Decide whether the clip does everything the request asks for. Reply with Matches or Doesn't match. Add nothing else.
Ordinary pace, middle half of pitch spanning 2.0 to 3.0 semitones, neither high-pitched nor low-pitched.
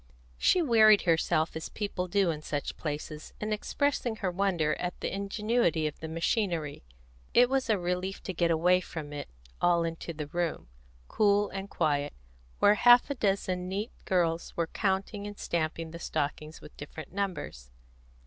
Doesn't match